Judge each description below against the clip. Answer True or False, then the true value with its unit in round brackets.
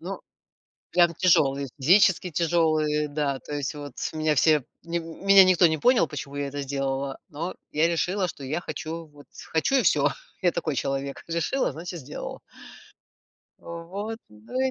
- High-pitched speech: False (155 Hz)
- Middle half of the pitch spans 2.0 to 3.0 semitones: False (3.4 semitones)